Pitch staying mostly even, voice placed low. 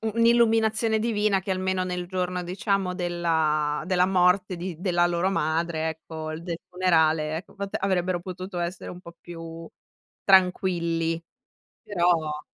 No: narrow, 2.3 semitones; medium, 180 Hz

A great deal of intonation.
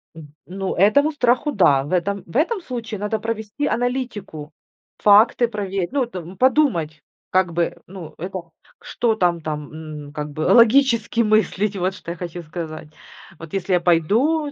Yes: wide, 5.9 semitones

